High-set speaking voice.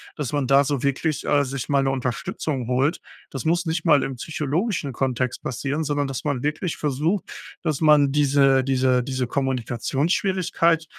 No: medium, 140 Hz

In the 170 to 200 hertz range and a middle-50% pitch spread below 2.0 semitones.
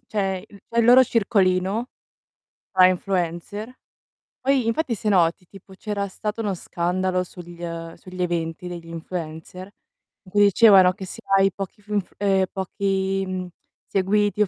No: high, 190 Hz; narrow, 2.4 semitones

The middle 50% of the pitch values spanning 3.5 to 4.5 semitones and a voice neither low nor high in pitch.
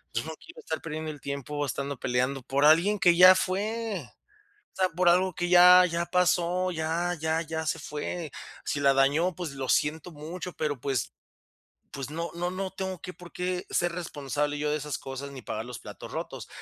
Yes: average, 4.0 semitones; medium, 160 Hz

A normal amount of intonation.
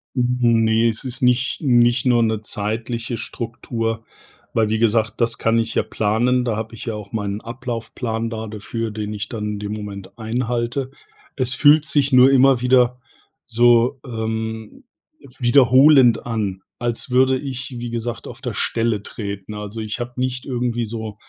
No: narrow, 2.1 semitones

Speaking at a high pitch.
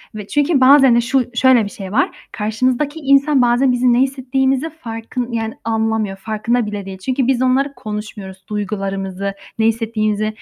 Yes: high, 235 Hz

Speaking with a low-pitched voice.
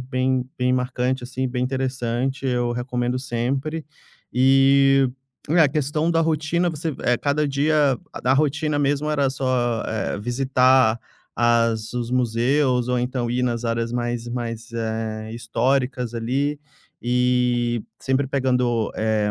Yes: low, 125 Hz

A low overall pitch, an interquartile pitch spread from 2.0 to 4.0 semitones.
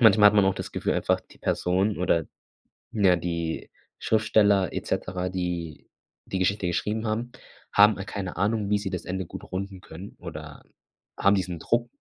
Yes: very low, 95 Hz; narrow, 2.6 semitones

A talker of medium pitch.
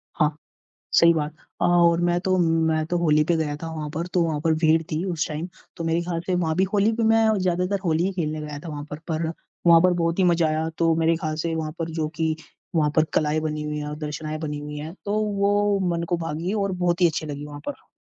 Yes: medium, 165 Hz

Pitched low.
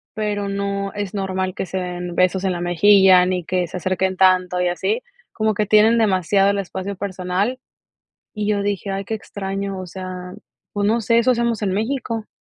No: high, 195 Hz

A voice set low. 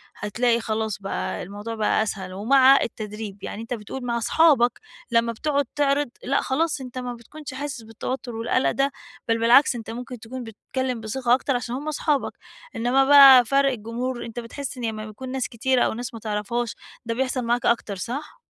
No: high, 240 Hz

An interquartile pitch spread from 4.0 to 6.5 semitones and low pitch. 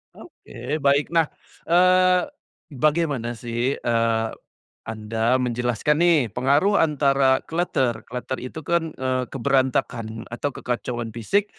Yes: average, 4.6 semitones; low, 130 Hz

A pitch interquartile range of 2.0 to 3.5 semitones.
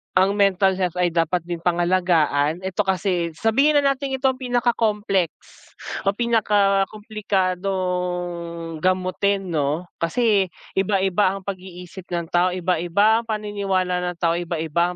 Yes: average, 2.8 semitones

